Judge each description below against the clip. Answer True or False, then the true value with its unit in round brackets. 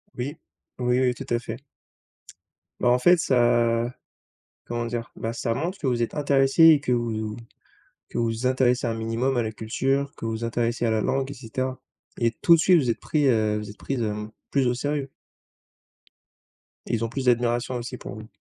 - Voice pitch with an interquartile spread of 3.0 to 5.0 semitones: False (2.6 semitones)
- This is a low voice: True (120 Hz)